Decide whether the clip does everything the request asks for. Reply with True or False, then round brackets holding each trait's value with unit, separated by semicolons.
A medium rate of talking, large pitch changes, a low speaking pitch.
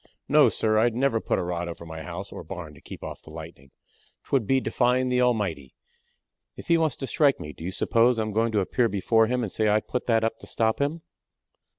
False (240 wpm; 5.8 semitones; 110 Hz)